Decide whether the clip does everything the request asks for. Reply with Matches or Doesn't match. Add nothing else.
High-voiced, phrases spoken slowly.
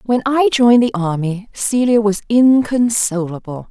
Matches